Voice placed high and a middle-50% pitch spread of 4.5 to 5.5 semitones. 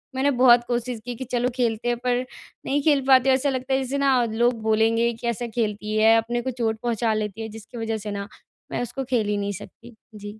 No: high, 235 Hz; narrow, 2.4 semitones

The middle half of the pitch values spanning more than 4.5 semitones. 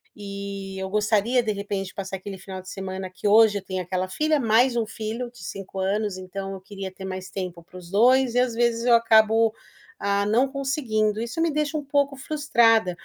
No: average, 3.8 semitones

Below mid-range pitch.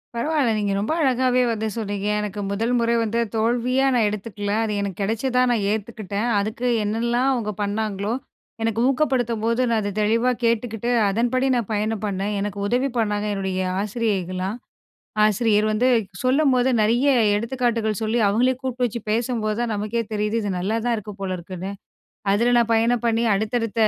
No: high, 225 Hz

